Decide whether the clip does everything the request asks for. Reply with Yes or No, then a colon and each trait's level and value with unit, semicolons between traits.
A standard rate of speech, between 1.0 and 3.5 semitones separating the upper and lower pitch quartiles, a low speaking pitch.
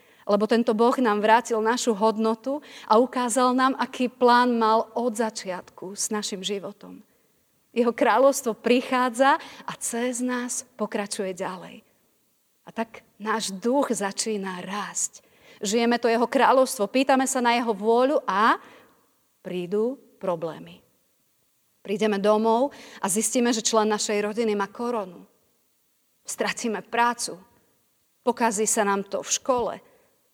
No: average, 125 wpm; average, 2.8 semitones; high, 230 Hz